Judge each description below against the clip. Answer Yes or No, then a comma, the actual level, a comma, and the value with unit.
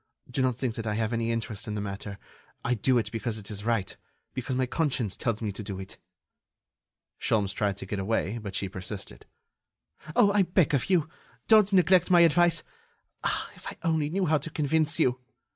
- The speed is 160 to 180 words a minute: No, average, 200 wpm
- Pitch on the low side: Yes, low, 120 Hz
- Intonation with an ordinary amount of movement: No, wide, 7.3 semitones